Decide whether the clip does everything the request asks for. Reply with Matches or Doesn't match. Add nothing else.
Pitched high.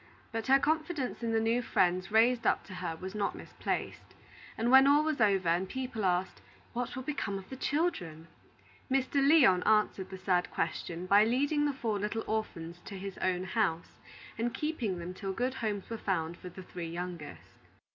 Matches